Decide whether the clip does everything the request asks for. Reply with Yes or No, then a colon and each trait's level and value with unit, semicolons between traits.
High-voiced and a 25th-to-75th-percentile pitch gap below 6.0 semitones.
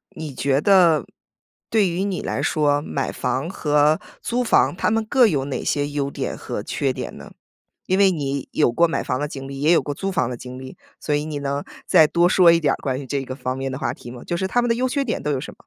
No: medium, 150 Hz; average, 5.1 semitones